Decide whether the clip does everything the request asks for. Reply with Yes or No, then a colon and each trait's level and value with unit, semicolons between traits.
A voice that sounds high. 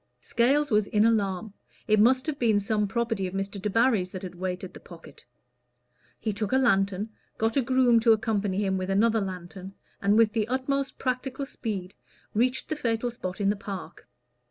Yes: high, 215 Hz